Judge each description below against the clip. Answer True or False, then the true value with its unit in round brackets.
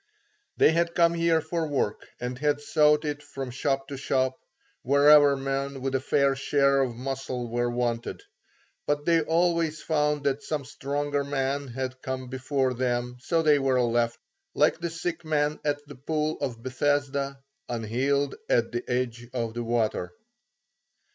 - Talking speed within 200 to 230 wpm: False (160 wpm)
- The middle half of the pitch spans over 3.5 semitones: False (2.7 semitones)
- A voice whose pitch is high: False (140 Hz)